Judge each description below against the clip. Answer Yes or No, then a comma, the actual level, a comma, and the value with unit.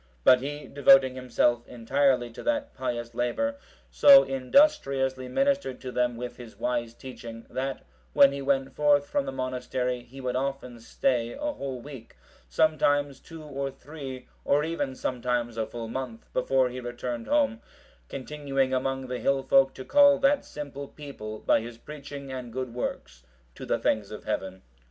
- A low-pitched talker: Yes, low, 130 Hz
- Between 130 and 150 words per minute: No, average, 165 wpm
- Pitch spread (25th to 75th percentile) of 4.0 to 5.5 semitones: No, average, 2.7 semitones